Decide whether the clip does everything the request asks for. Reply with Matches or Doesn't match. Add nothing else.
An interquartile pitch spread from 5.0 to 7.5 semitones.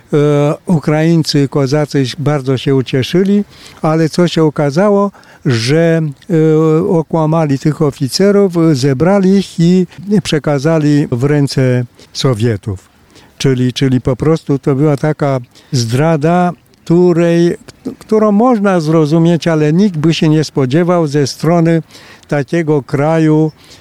Doesn't match